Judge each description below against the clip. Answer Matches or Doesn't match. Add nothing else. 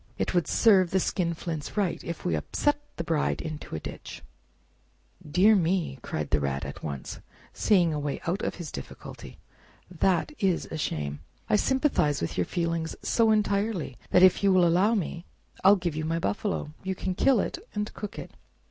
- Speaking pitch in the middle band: Matches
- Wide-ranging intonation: Doesn't match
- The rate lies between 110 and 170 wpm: Doesn't match